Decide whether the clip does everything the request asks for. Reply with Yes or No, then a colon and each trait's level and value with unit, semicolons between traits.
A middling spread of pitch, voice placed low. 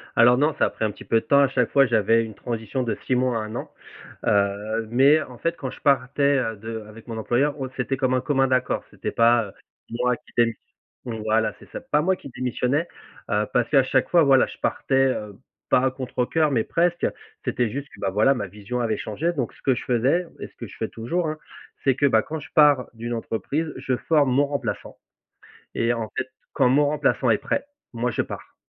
Yes: average, 3.7 semitones; low, 125 Hz